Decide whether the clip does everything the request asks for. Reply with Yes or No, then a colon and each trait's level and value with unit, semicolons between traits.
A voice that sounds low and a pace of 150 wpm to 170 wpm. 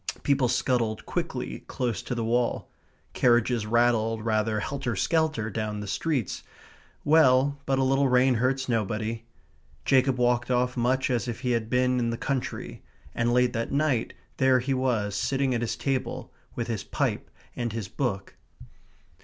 Yes: low, 120 Hz; average, 160 wpm